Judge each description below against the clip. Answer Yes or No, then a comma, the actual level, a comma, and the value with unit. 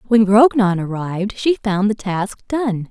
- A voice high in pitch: Yes, high, 210 Hz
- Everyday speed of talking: Yes, average, 165 wpm